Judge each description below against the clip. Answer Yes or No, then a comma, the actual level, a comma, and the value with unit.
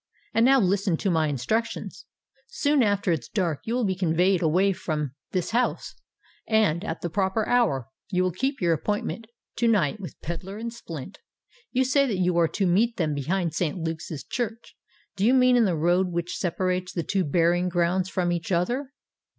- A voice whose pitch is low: No, medium, 185 Hz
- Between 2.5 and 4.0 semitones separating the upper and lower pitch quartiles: No, average, 4.5 semitones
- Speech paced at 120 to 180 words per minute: No, average, 190 wpm